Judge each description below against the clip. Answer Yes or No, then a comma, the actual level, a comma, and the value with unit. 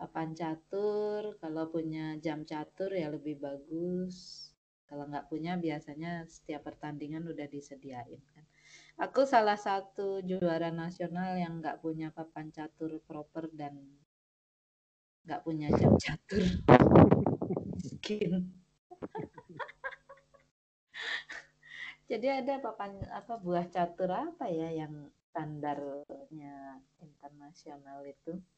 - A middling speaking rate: Yes, average, 95 wpm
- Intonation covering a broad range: No, average, 3.4 semitones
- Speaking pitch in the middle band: Yes, medium, 160 Hz